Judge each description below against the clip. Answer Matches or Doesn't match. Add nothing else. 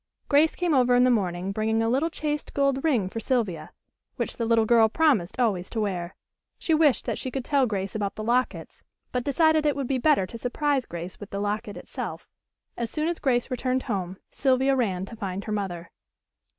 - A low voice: Doesn't match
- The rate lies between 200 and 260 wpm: Matches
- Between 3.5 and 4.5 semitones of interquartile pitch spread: Doesn't match